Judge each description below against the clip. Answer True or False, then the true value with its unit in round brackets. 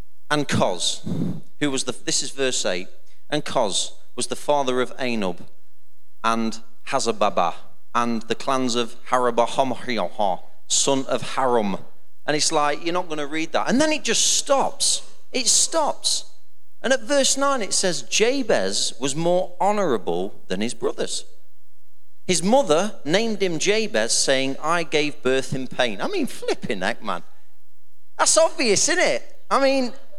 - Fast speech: False (155 wpm)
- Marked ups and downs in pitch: True (8.7 semitones)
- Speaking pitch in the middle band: True (155 Hz)